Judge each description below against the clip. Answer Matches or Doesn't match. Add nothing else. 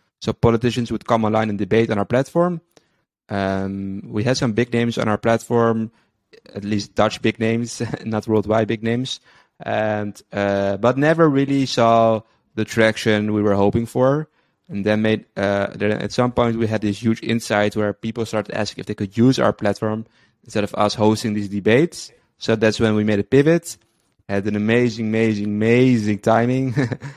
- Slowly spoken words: Doesn't match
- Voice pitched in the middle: Doesn't match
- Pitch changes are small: Matches